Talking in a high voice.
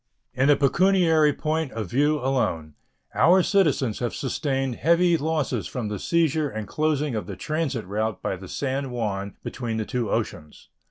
No: low, 135 Hz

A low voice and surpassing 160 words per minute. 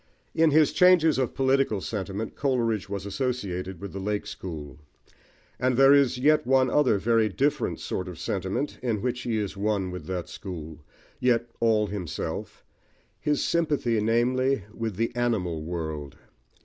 No: low, 115 Hz; average, 150 wpm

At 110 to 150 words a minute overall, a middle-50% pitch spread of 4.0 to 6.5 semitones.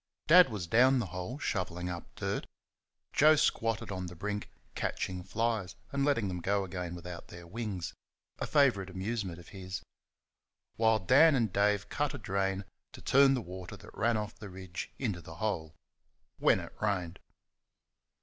No: average, 170 wpm; average, 4.3 semitones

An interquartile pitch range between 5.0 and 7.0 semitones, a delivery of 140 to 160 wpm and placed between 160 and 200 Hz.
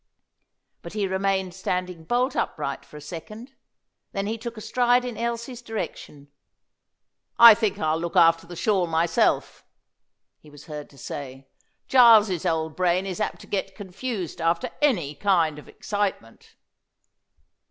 Yes: average, 5.3 semitones; average, 145 wpm; high, 190 Hz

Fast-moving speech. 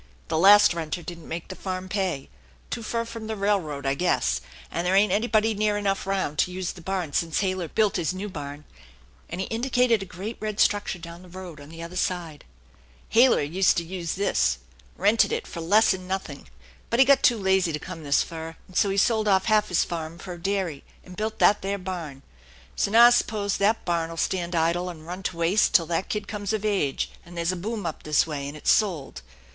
Yes: fast, 220 wpm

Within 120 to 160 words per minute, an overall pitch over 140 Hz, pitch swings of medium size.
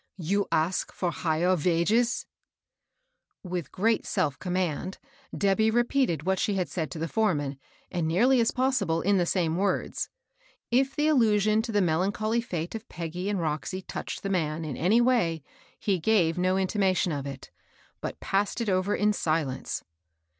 No: average, 170 wpm; medium, 185 Hz; average, 4.6 semitones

